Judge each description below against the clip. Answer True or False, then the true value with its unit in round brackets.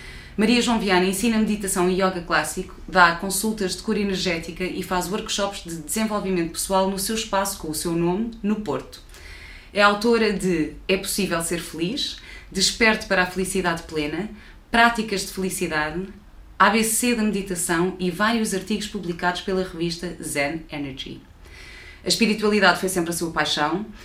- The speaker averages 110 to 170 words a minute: True (150 wpm)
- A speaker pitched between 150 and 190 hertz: True (185 Hz)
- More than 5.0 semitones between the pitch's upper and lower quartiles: False (3.4 semitones)